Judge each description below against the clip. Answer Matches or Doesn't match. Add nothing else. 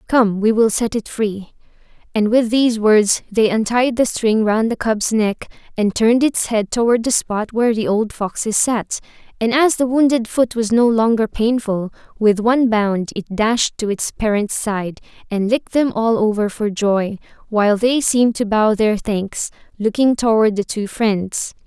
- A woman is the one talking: Matches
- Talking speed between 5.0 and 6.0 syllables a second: Doesn't match